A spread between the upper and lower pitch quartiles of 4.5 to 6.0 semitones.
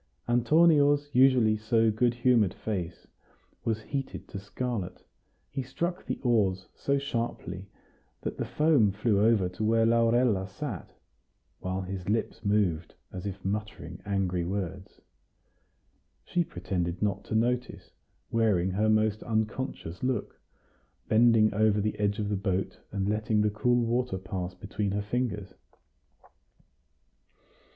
No: average, 3.7 semitones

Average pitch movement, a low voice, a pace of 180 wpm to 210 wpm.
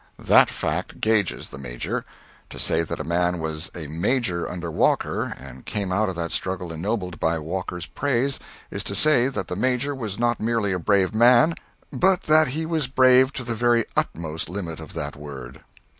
No: wide, 6.9 semitones; low, 100 Hz; average, 190 wpm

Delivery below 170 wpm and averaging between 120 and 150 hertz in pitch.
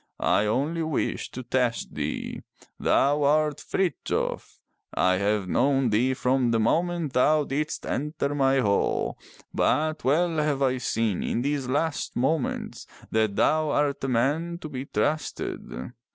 Yes: average, 140 wpm; low, 135 Hz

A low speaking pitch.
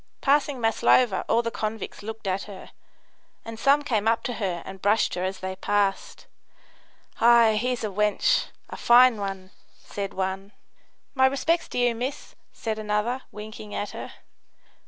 No: high, 220 Hz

